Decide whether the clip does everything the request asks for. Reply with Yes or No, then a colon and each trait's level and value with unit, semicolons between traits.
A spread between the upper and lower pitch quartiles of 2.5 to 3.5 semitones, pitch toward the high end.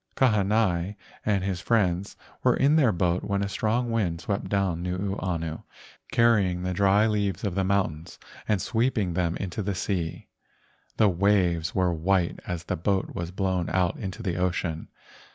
No: average, 2.8 semitones; very low, 95 Hz